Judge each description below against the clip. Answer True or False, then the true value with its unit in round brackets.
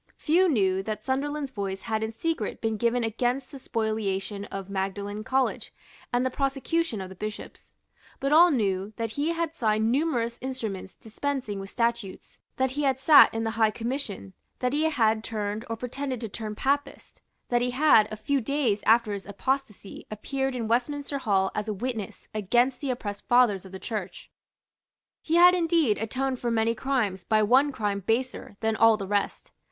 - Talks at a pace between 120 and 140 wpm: False (180 wpm)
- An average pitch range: True (4.2 semitones)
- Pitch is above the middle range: True (230 Hz)